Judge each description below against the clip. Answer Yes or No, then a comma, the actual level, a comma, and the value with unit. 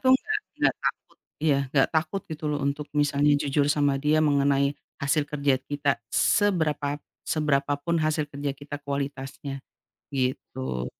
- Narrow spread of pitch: Yes, narrow, 1.5 semitones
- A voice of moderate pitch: Yes, medium, 145 Hz